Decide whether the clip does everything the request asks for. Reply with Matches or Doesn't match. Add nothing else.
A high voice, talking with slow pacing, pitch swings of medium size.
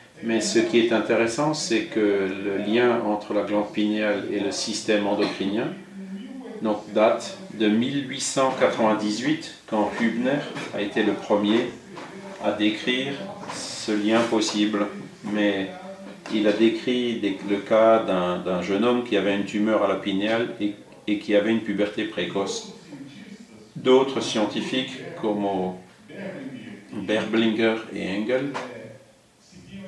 Doesn't match